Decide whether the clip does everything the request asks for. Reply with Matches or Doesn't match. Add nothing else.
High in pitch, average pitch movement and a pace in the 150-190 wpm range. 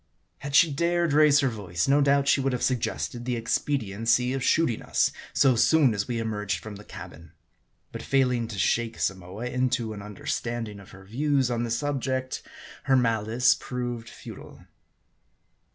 Doesn't match